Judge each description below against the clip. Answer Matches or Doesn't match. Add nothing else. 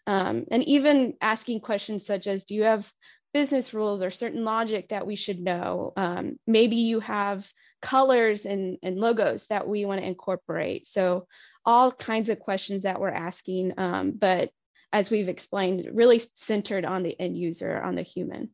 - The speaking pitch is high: Matches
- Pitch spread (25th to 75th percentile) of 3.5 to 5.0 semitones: Doesn't match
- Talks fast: Doesn't match